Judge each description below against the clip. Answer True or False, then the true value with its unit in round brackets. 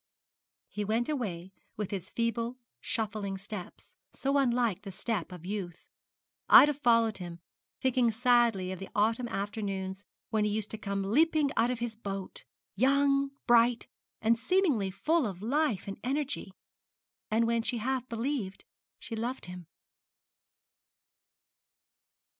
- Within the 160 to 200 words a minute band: False (135 wpm)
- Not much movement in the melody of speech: False (4.0 semitones)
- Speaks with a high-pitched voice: True (225 Hz)